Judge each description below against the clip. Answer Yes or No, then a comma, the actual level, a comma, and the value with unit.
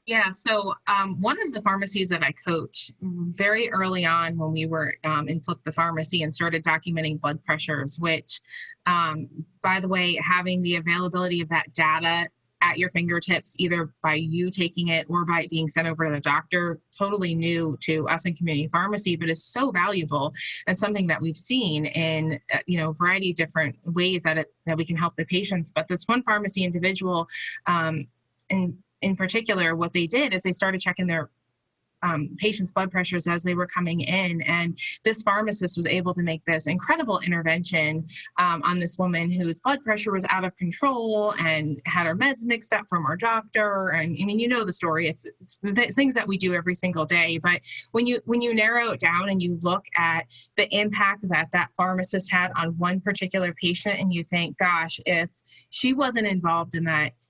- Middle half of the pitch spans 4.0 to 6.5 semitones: No, average, 2.9 semitones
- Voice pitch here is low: No, medium, 175 Hz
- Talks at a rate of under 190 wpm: No, average, 200 wpm